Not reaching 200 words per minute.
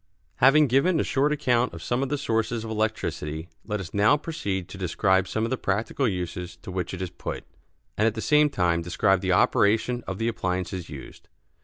No: fast, 205 wpm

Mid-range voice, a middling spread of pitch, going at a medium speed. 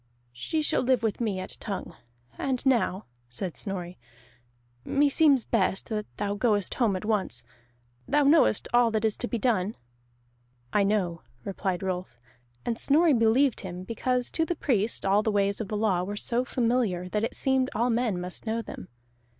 No: high, 220 Hz; average, 4.4 semitones; average, 175 wpm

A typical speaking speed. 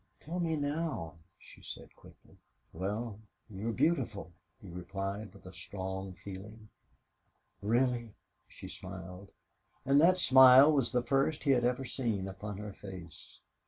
No: slow, 130 wpm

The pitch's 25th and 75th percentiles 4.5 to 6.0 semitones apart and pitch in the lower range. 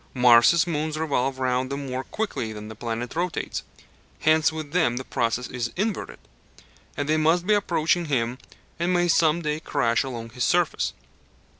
No: average, 5.1 semitones; medium, 145 Hz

